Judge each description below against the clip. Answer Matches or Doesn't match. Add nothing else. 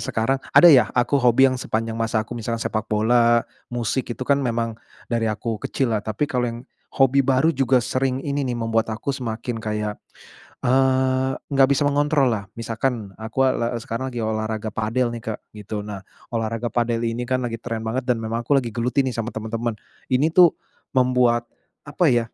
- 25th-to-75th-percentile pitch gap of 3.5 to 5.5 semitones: Doesn't match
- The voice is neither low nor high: Doesn't match